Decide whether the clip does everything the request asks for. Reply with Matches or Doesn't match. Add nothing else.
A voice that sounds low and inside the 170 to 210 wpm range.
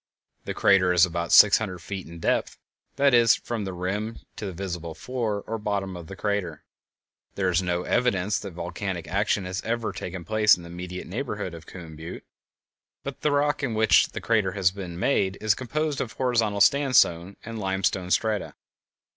Matches